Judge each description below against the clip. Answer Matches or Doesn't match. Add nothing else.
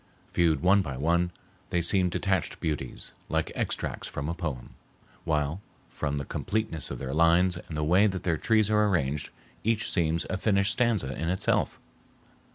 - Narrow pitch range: Doesn't match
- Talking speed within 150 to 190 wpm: Matches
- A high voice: Doesn't match